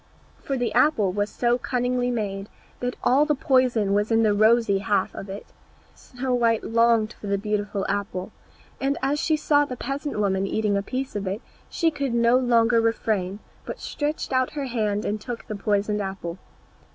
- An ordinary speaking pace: Yes, average, 185 wpm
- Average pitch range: Yes, average, 3.8 semitones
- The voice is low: No, high, 230 Hz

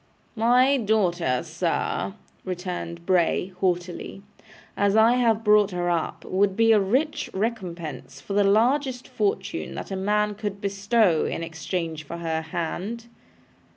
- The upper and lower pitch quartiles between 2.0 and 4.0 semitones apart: No, average, 4.4 semitones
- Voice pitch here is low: No, high, 195 Hz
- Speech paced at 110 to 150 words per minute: Yes, slow, 135 wpm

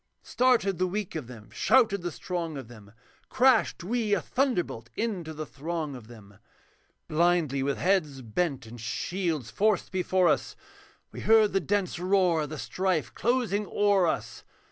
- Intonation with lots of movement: Yes, wide, 6.2 semitones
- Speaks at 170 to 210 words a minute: No, average, 160 wpm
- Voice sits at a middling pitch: Yes, medium, 175 Hz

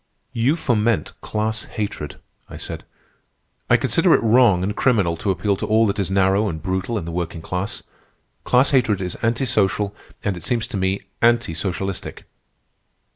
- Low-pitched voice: Yes, low, 100 Hz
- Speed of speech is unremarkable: Yes, average, 170 wpm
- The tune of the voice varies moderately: Yes, average, 3.4 semitones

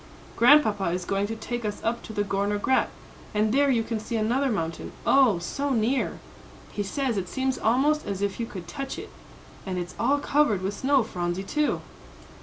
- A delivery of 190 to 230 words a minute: Yes, average, 195 wpm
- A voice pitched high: Yes, high, 220 Hz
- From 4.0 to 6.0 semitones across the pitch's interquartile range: Yes, average, 5.1 semitones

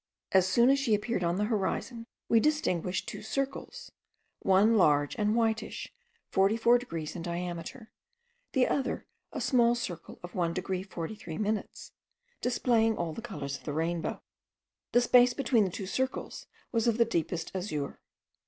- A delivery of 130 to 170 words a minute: Yes, average, 160 wpm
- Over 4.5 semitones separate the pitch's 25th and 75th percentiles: Yes, wide, 5.4 semitones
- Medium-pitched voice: No, high, 210 Hz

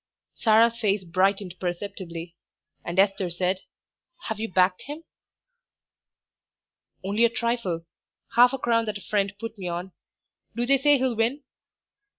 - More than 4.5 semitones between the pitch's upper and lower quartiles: No, average, 4.1 semitones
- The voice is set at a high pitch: Yes, high, 205 Hz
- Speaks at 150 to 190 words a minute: No, average, 140 wpm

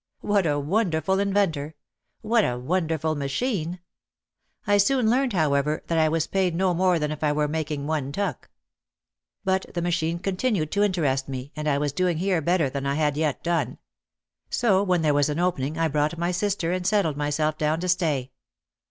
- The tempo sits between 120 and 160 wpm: No, average, 195 wpm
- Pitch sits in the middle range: Yes, medium, 160 Hz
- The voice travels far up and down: No, average, 4.1 semitones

